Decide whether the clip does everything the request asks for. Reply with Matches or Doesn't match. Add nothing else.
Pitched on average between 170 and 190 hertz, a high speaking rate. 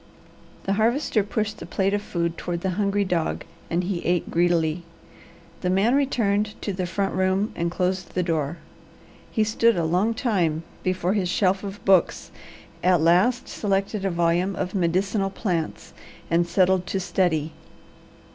Doesn't match